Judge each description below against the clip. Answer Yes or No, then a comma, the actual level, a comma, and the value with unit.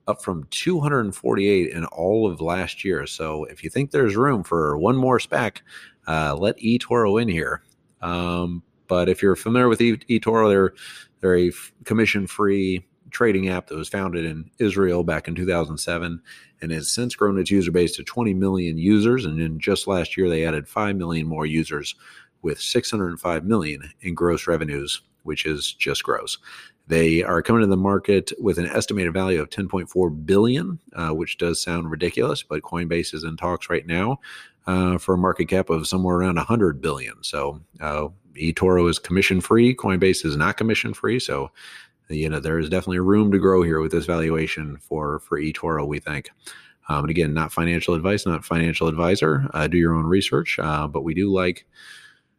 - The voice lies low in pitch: Yes, very low, 90 Hz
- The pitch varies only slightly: No, average, 3.4 semitones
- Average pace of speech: Yes, average, 185 wpm